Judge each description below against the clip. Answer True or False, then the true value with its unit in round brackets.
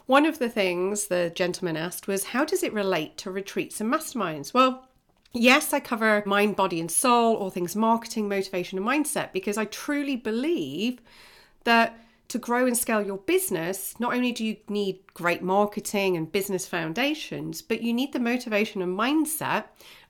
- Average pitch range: True (4.5 semitones)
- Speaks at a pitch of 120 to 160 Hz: False (215 Hz)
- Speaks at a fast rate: False (175 wpm)